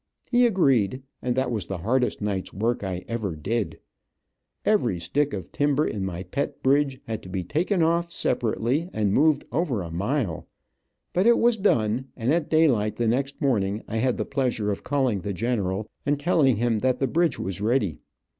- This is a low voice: Yes, low, 120 Hz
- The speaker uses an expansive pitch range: Yes, wide, 5.9 semitones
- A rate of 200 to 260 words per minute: No, average, 185 wpm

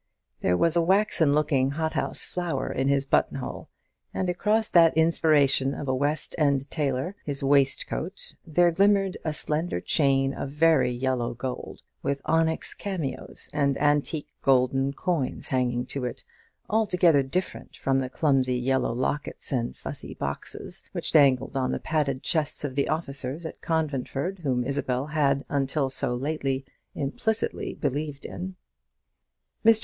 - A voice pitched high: No, medium, 140 Hz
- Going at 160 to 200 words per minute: No, average, 145 wpm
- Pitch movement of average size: Yes, average, 3.3 semitones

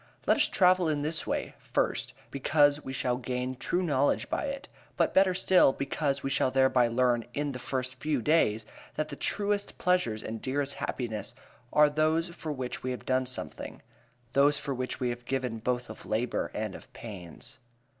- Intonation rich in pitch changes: No, average, 3.6 semitones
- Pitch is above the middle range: No, low, 135 Hz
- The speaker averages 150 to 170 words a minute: No, average, 185 wpm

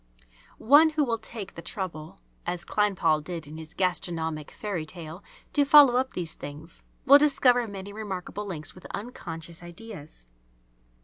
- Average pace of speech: Yes, average, 145 wpm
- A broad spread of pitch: Yes, wide, 5.9 semitones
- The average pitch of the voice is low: No, medium, 185 Hz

